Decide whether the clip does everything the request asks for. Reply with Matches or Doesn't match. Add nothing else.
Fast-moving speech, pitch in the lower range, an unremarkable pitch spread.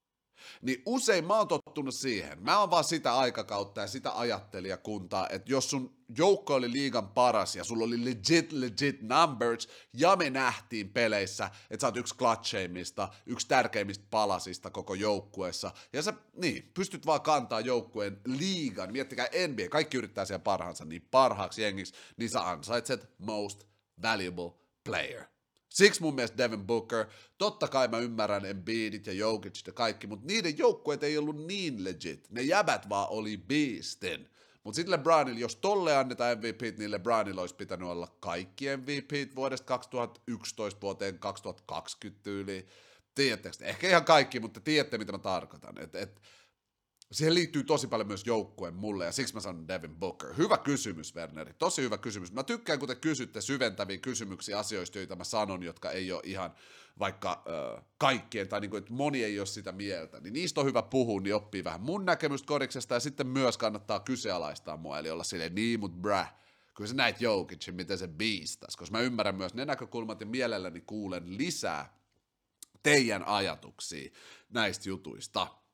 Doesn't match